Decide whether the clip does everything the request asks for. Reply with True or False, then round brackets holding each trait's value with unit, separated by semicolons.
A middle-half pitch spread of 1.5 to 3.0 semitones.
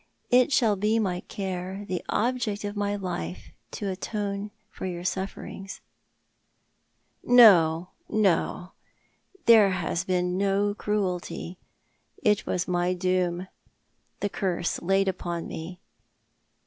True (2.4 semitones)